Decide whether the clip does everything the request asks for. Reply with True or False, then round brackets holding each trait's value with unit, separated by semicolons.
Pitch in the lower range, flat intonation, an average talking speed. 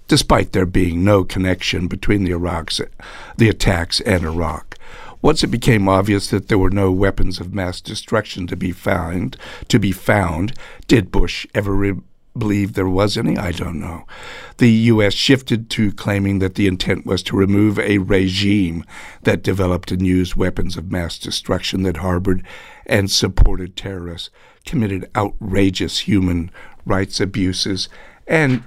True (95 Hz; 2.0 semitones; 155 wpm)